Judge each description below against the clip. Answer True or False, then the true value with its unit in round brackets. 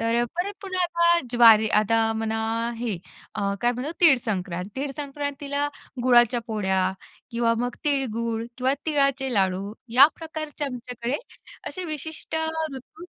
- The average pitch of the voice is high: True (250 Hz)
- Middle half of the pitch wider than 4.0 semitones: True (4.5 semitones)